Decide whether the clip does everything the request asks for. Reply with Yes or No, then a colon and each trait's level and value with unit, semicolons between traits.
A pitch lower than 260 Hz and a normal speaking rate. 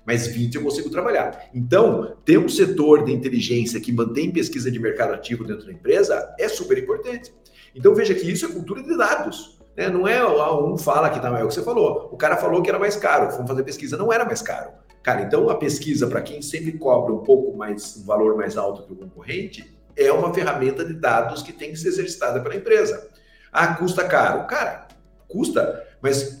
No: high, 190 Hz; fast, 210 wpm